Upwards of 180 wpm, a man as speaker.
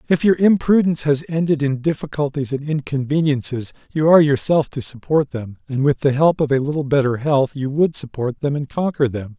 Yes: average, 200 wpm; male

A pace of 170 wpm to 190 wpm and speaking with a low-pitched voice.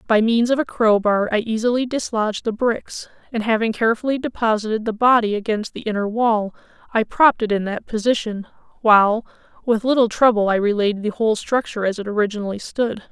No: average, 180 wpm; high, 220 Hz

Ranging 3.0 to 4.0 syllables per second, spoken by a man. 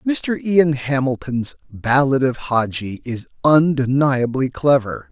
Yes: 3.9 syllables/s; male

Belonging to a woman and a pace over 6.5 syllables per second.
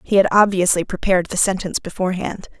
Yes: female; 6.7 syllables/s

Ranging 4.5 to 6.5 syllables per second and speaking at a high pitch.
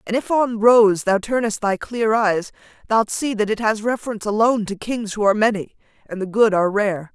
Yes: 5.4 syllables/s; high, 215 Hz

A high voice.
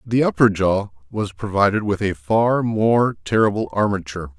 No: low, 100 Hz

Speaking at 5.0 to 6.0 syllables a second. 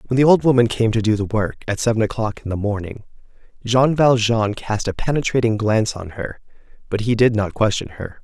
Yes: 5.7 syllables/s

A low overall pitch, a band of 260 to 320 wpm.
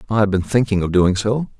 Yes: low, 105 Hz; fast, 265 wpm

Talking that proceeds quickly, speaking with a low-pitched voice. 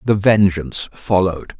No: slow, 115 wpm; very low, 95 Hz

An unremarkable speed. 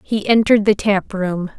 Yes: average, 190 wpm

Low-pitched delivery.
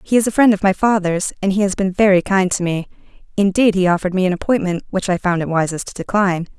No: high, 190 Hz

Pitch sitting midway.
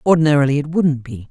Yes: medium, 145 Hz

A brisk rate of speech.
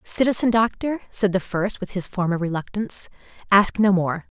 No: average, 165 wpm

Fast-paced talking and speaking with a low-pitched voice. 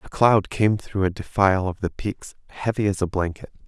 Yes: fast, 210 wpm; very low, 95 Hz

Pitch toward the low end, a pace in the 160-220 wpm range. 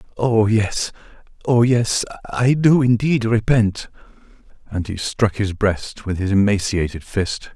No: low, 110 Hz; slow, 135 wpm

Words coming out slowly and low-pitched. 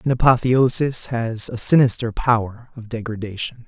Yes: slow, 130 wpm; low, 120 Hz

